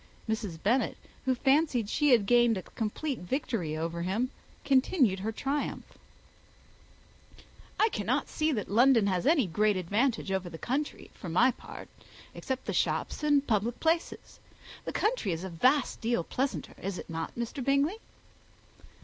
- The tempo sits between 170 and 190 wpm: No, average, 150 wpm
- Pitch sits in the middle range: No, high, 235 Hz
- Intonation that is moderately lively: No, wide, 6.1 semitones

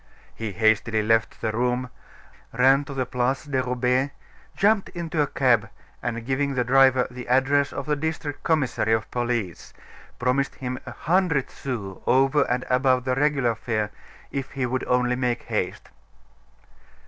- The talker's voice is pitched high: No, low, 125 Hz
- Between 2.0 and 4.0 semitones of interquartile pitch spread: Yes, narrow, 2.5 semitones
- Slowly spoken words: No, average, 155 wpm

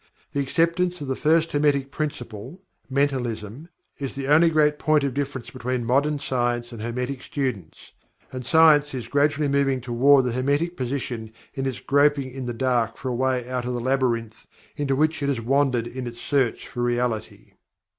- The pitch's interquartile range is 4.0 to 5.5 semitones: No, average, 3.0 semitones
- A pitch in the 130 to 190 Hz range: Yes, low, 135 Hz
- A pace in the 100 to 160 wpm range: No, average, 175 wpm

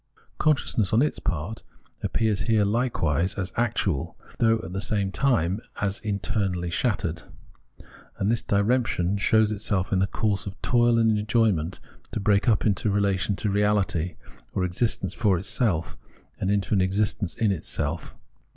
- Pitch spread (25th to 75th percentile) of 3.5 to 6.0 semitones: No, average, 3.0 semitones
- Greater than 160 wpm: No, average, 150 wpm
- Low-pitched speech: Yes, low, 100 Hz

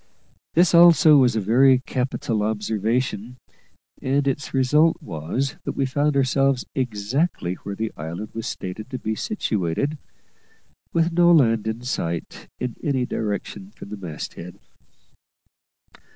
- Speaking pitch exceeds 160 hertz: No, low, 125 Hz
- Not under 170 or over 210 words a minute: No, slow, 135 wpm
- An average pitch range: Yes, average, 4.9 semitones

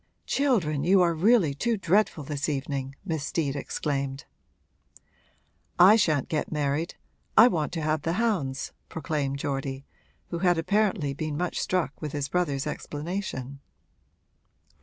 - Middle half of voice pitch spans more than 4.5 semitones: No, average, 4.2 semitones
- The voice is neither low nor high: Yes, medium, 155 Hz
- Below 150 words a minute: Yes, slow, 135 wpm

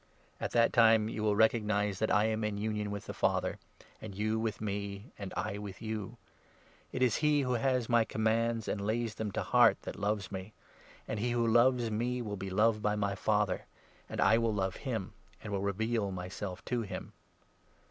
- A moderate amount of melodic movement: No, narrow, 2.2 semitones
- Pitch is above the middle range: No, low, 110 Hz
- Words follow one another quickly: Yes, fast, 210 wpm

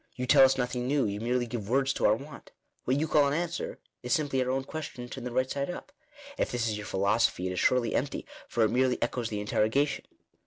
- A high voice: No, low, 125 Hz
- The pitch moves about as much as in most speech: Yes, average, 3.3 semitones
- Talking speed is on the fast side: Yes, fast, 240 wpm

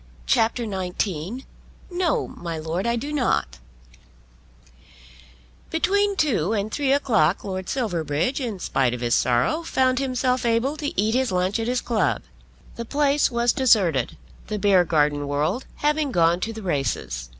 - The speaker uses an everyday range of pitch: No, wide, 7.9 semitones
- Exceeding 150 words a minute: No, average, 145 wpm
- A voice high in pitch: Yes, high, 220 Hz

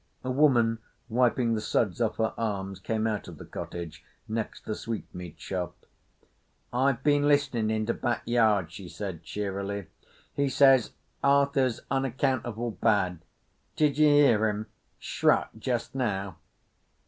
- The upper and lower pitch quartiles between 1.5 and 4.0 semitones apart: No, average, 4.5 semitones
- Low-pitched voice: Yes, low, 115 Hz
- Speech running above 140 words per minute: No, slow, 135 wpm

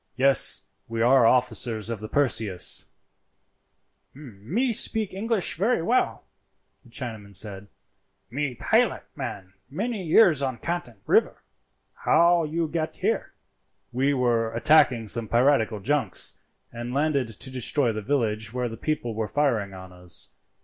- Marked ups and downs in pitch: Yes, wide, 5.7 semitones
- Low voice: Yes, low, 125 Hz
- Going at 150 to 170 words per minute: No, slow, 135 wpm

